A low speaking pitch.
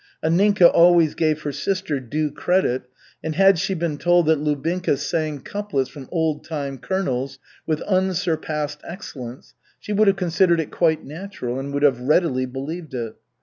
No: medium, 155 Hz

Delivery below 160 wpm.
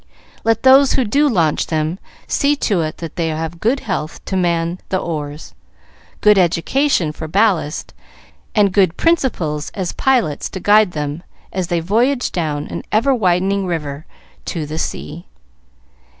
Yes: average, 150 wpm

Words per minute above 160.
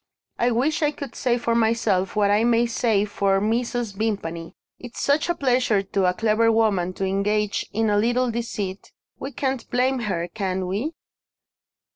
Yes: average, 170 wpm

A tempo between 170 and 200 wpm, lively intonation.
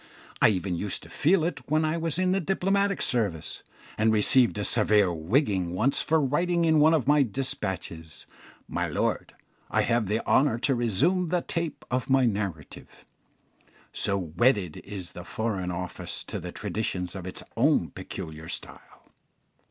No: average, 160 wpm; wide, 8.8 semitones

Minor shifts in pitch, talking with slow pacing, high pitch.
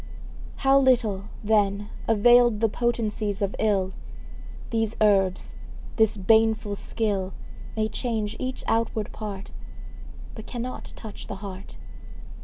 Yes: narrow, 2.2 semitones; slow, 110 wpm; high, 215 Hz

